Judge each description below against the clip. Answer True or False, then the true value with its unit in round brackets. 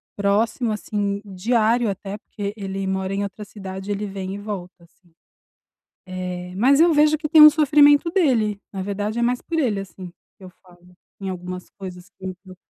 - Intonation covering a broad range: False (3.7 semitones)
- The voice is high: True (200 Hz)